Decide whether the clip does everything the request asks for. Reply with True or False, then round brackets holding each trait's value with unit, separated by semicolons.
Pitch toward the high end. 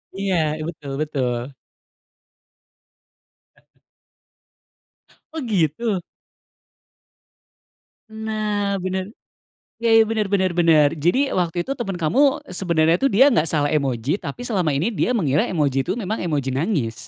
False (180 Hz)